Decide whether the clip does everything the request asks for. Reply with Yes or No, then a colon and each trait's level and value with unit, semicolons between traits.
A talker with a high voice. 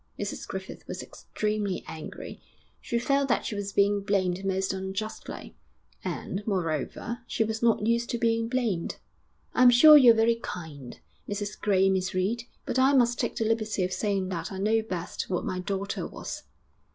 Yes: high, 205 Hz